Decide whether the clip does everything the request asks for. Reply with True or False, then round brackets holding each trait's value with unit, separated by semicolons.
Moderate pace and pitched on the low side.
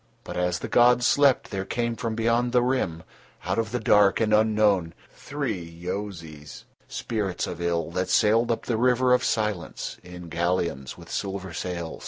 True (170 wpm; 100 Hz)